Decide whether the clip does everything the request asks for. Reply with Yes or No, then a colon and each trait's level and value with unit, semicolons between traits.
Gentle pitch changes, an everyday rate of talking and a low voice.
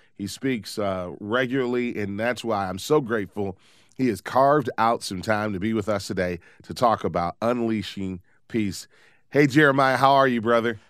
No: average, 3.8 semitones; average, 175 wpm; low, 110 Hz